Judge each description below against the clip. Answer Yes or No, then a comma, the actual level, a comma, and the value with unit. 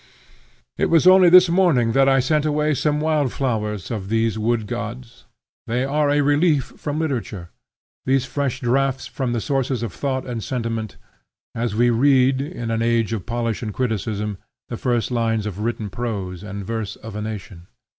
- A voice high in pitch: No, low, 120 Hz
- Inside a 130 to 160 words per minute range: No, average, 175 wpm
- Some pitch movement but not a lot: Yes, average, 3.8 semitones